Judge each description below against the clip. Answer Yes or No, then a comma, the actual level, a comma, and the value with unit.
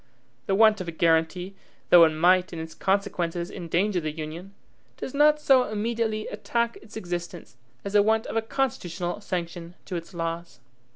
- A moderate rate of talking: Yes, average, 170 wpm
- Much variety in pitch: No, average, 4.2 semitones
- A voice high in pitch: No, medium, 180 Hz